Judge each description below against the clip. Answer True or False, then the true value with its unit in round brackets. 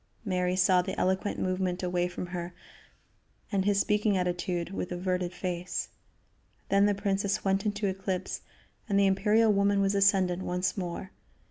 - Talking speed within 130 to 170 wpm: True (150 wpm)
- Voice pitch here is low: False (190 Hz)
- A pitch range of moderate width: False (1.8 semitones)